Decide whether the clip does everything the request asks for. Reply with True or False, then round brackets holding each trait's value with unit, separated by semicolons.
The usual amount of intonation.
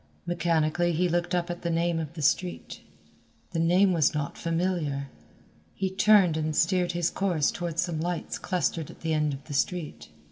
False (2.2 semitones)